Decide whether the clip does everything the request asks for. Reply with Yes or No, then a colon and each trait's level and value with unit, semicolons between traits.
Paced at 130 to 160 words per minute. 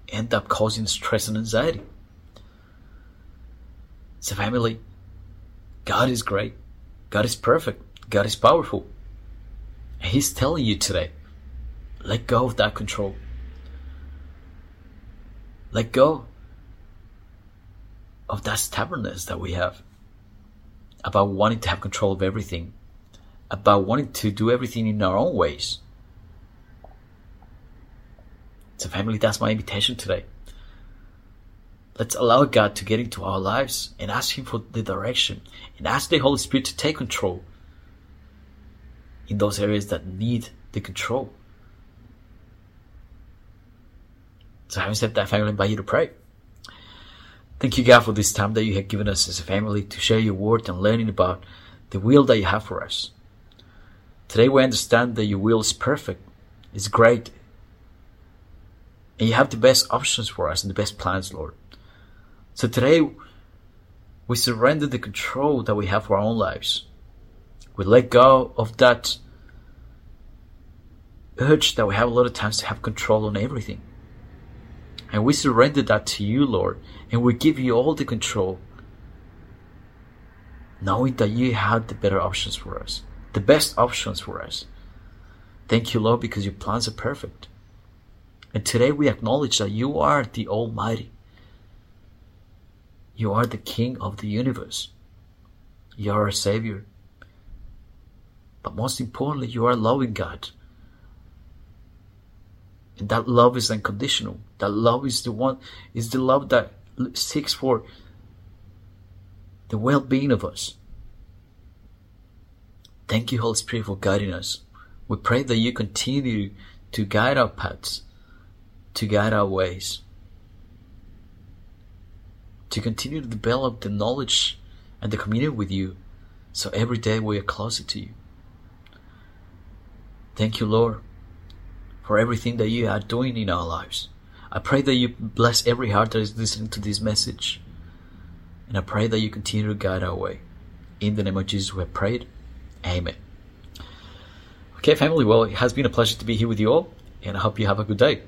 Yes: average, 150 wpm